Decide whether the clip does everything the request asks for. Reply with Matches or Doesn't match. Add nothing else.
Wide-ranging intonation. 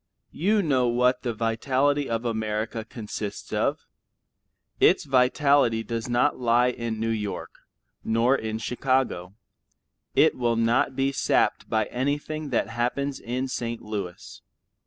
Doesn't match